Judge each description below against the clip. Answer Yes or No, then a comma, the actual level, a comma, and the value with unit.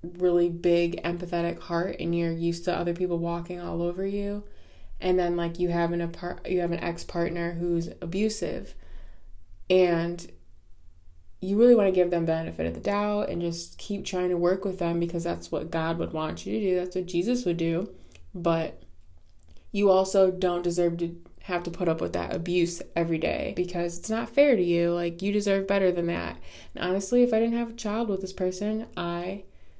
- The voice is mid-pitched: Yes, medium, 175 Hz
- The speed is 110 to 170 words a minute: No, average, 200 wpm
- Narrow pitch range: Yes, narrow, 1.8 semitones